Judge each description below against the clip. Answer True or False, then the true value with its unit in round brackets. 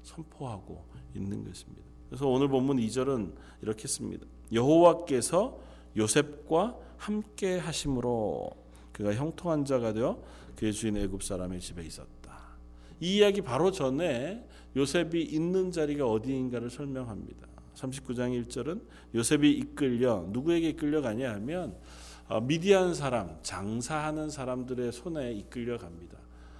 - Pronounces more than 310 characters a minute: False (290 characters per minute)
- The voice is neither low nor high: False (125 Hz)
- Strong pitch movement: True (8.8 semitones)